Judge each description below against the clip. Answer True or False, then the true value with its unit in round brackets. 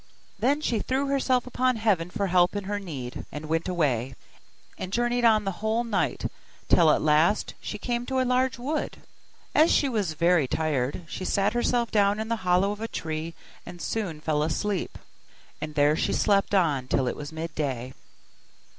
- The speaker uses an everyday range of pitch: False (6.8 semitones)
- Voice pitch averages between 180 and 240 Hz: True (190 Hz)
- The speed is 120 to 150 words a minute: False (180 wpm)